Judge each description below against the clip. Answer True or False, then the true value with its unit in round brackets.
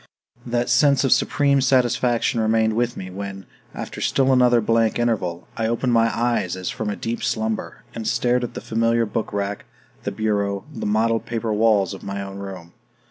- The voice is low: True (115 Hz)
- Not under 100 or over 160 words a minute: False (185 wpm)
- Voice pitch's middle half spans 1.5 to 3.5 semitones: True (2.8 semitones)